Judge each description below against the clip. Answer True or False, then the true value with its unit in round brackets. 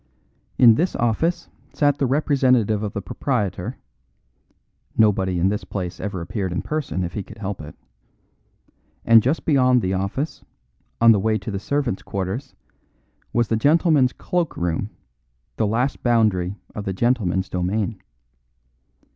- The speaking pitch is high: False (110 Hz)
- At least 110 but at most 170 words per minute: True (145 wpm)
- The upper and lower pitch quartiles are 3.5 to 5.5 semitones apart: True (5.2 semitones)